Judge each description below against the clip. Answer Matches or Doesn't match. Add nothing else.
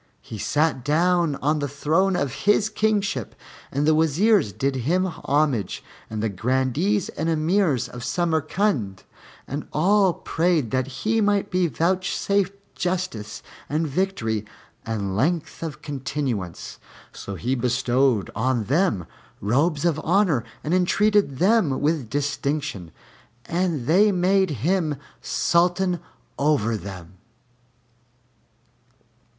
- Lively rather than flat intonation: Matches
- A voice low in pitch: Doesn't match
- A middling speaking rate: Doesn't match